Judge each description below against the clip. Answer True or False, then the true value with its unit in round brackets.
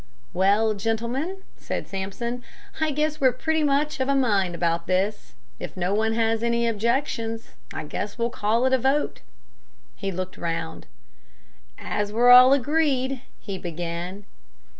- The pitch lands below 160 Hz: False (225 Hz)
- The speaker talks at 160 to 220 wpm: False (150 wpm)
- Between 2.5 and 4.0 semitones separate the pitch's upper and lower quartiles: False (5.2 semitones)